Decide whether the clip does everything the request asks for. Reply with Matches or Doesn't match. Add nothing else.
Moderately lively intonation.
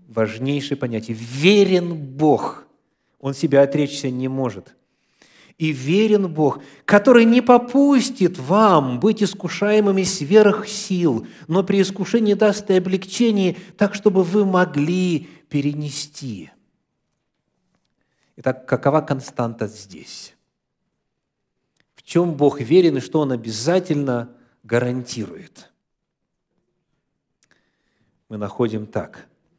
Doesn't match